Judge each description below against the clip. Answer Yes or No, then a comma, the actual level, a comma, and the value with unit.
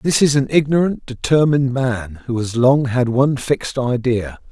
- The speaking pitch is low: Yes, low, 130 Hz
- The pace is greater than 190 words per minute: No, average, 175 wpm